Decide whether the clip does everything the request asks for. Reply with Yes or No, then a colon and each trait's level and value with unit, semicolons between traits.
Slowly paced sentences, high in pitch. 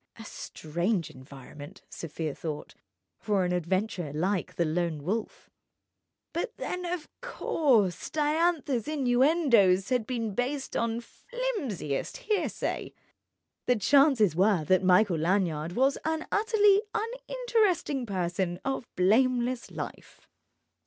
Yes: slow, 105 wpm; high, 225 Hz